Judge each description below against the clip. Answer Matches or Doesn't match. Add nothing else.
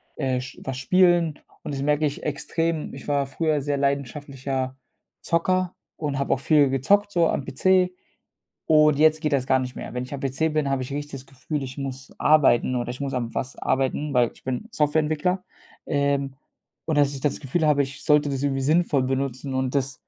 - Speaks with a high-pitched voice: Doesn't match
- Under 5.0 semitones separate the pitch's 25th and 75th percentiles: Matches